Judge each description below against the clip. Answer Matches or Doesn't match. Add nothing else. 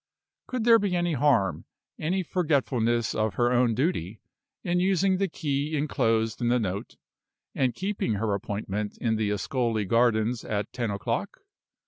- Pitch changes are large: Matches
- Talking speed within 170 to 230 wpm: Doesn't match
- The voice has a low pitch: Matches